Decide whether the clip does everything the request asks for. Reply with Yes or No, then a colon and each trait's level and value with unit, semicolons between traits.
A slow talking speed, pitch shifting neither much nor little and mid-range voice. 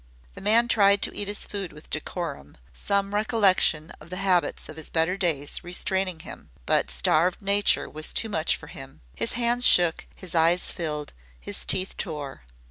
No: average, 170 wpm; average, 4.1 semitones; medium, 180 Hz